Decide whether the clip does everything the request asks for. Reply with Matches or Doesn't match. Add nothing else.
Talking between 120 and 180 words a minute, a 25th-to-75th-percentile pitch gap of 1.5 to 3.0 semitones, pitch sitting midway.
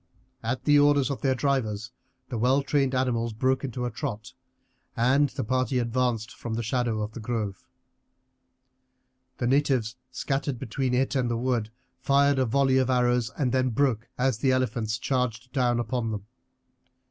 Doesn't match